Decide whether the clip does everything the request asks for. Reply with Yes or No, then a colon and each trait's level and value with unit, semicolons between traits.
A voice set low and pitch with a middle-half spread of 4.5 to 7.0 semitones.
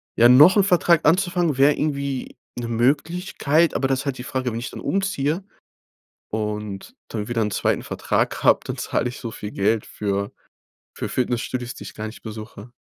Yes: low, 125 Hz; wide, 5.5 semitones